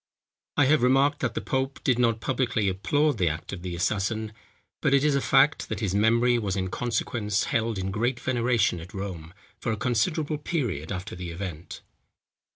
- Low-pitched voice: Yes, low, 115 Hz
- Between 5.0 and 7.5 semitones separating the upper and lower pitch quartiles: Yes, wide, 5.4 semitones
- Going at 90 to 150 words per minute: No, average, 185 wpm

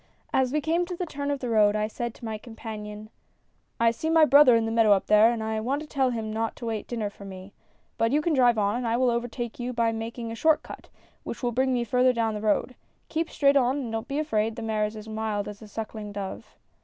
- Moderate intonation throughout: Yes, average, 3.0 semitones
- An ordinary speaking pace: No, fast, 280 wpm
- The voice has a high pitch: Yes, high, 230 Hz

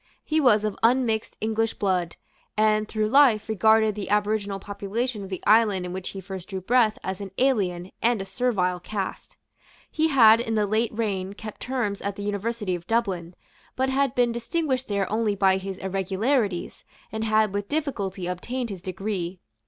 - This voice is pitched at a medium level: No, high, 210 Hz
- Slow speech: No, average, 175 wpm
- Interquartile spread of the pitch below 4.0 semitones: Yes, average, 3.3 semitones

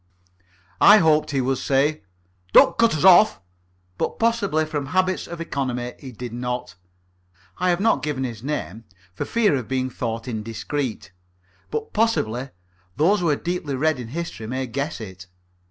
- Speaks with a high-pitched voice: No, medium, 140 Hz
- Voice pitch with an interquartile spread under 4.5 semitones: No, wide, 5.5 semitones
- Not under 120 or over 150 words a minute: No, average, 160 wpm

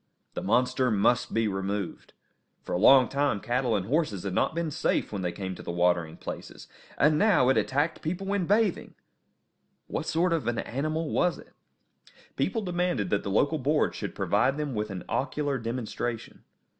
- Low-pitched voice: Yes, low, 125 Hz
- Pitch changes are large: Yes, wide, 7.2 semitones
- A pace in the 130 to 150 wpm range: No, average, 180 wpm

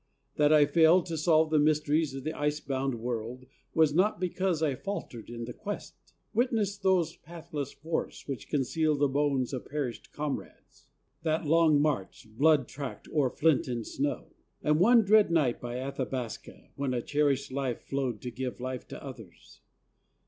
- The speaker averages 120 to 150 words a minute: No, average, 165 wpm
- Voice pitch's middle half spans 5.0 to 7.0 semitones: No, average, 3.7 semitones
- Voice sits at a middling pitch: Yes, medium, 145 Hz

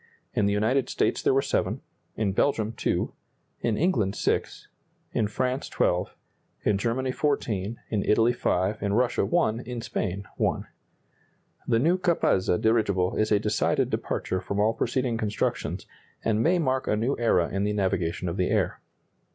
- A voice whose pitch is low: Yes, low, 110 Hz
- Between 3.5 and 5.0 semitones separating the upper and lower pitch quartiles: Yes, average, 4.0 semitones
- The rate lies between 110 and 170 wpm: Yes, average, 160 wpm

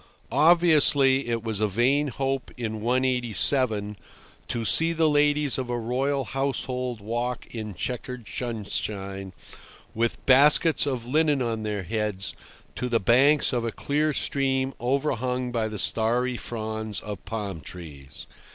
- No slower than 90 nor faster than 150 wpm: Yes, slow, 135 wpm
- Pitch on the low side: Yes, low, 120 Hz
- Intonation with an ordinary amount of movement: Yes, average, 3.7 semitones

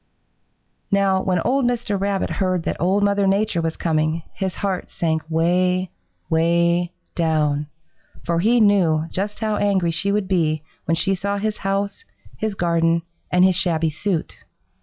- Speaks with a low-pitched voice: No, medium, 185 Hz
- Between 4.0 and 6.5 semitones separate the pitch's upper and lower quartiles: No, average, 3.3 semitones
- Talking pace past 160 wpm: No, average, 155 wpm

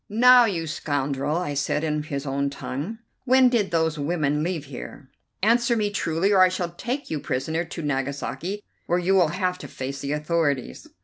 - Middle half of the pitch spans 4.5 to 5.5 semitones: Yes, average, 5.1 semitones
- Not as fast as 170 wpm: No, average, 185 wpm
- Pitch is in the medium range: Yes, medium, 165 Hz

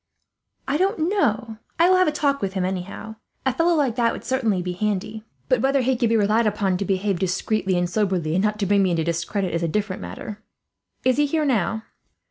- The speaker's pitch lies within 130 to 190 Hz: No, high, 210 Hz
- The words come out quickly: Yes, fast, 225 wpm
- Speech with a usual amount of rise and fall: No, wide, 5.8 semitones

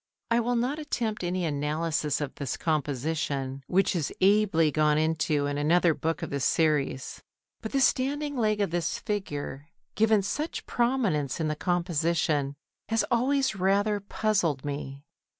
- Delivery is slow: No, average, 150 wpm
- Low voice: No, medium, 170 Hz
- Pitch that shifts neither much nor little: No, wide, 6.4 semitones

